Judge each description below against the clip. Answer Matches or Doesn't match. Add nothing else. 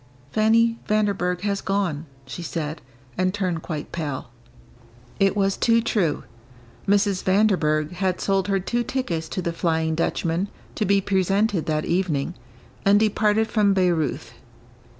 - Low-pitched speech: Doesn't match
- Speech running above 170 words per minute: Doesn't match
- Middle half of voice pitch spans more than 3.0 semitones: Matches